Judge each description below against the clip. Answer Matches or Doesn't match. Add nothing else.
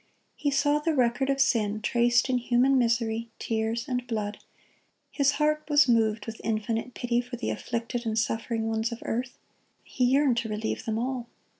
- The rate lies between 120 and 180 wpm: Matches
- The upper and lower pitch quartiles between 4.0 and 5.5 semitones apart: Doesn't match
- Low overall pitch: Doesn't match